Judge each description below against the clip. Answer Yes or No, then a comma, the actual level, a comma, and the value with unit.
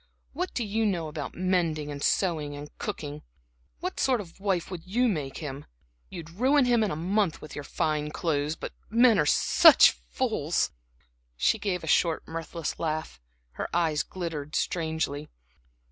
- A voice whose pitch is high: No, medium, 165 Hz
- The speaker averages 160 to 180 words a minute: Yes, average, 165 wpm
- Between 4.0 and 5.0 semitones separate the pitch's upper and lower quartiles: Yes, average, 4.7 semitones